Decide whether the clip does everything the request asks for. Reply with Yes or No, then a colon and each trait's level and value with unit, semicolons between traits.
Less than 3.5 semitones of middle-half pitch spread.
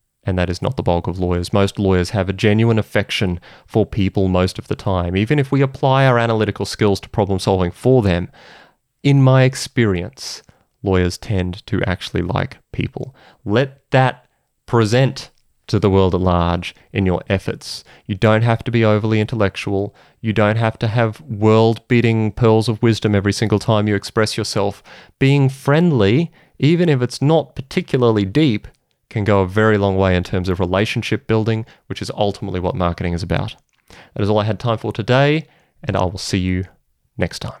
No: average, 4.0 semitones